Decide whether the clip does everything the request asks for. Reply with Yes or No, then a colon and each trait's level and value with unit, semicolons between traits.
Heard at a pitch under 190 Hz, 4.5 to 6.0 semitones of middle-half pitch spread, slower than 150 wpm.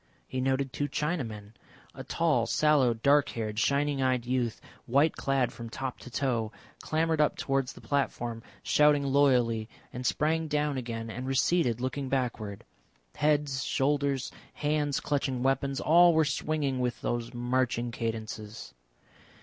No: low, 135 Hz; average, 3.3 semitones; average, 140 wpm